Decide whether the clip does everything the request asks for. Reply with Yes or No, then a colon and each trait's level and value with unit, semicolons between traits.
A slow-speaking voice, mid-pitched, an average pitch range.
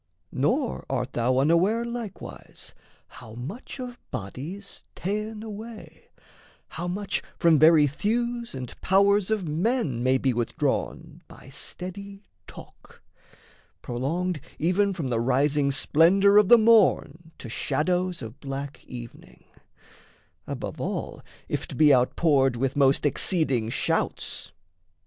No: slow, 120 wpm; medium, 165 Hz; wide, 7.1 semitones